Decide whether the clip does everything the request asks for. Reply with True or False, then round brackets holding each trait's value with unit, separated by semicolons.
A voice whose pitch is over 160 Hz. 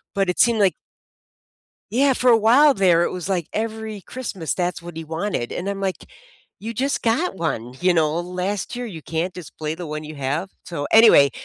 True (185 Hz)